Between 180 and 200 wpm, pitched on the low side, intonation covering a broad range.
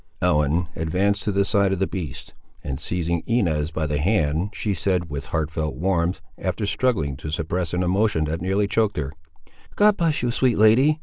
No: average, 185 wpm; very low, 90 Hz; average, 4.6 semitones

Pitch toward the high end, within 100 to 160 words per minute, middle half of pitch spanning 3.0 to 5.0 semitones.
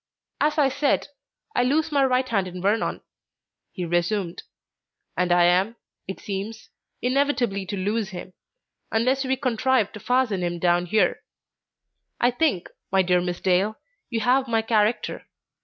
No: high, 215 Hz; average, 150 wpm; wide, 5.6 semitones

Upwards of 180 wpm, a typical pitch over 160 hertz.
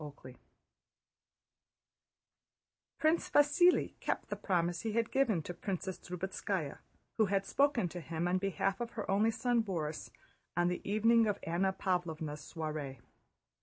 No: average, 140 wpm; high, 190 Hz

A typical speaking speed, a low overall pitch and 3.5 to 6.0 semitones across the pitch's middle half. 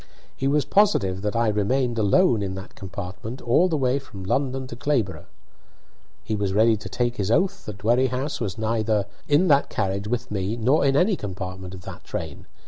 Yes: average, 190 wpm; low, 115 Hz; average, 5.3 semitones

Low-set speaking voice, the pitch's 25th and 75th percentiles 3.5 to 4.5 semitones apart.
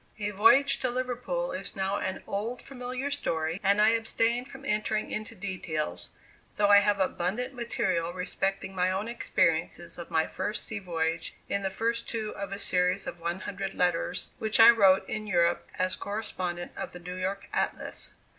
No: high, 200 Hz; average, 4.0 semitones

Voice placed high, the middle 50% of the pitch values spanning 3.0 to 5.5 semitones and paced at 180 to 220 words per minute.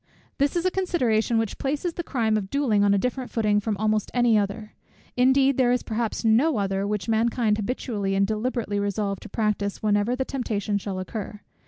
Yes: high, 220 Hz; average, 3.5 semitones; average, 190 wpm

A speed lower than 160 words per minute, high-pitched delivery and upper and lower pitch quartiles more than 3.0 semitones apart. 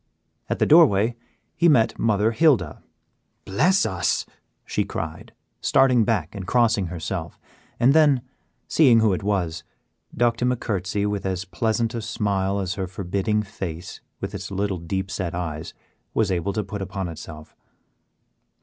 No: average, 150 wpm; low, 100 Hz; average, 3.8 semitones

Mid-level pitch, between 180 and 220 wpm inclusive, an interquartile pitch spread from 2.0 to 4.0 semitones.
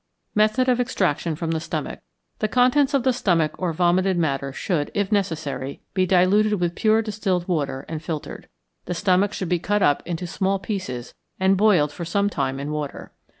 No: medium, 180 Hz; average, 185 wpm; average, 4.5 semitones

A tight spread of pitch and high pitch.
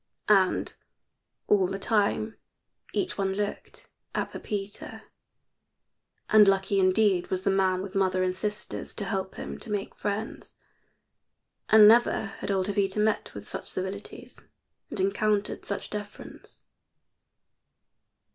Yes: narrow, 1.6 semitones; high, 200 Hz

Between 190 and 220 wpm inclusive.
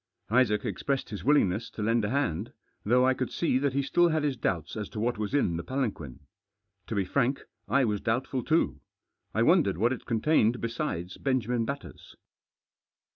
No: average, 180 wpm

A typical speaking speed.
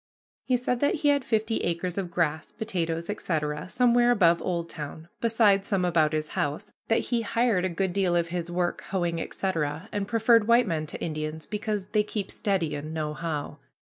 Yes: average, 185 wpm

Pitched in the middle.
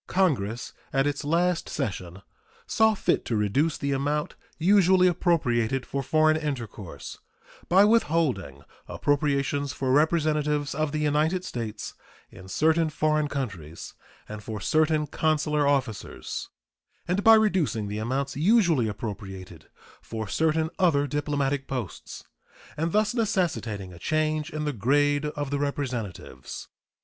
Yes: medium, 145 Hz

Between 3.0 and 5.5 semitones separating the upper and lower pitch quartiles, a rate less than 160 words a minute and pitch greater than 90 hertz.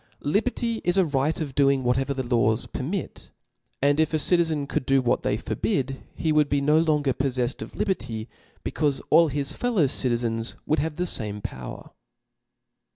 No: average, 4.2 semitones; average, 185 wpm; medium, 140 Hz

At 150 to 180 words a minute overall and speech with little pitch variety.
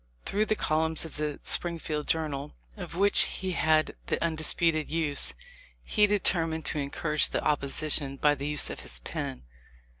Yes: average, 155 wpm; narrow, 2.0 semitones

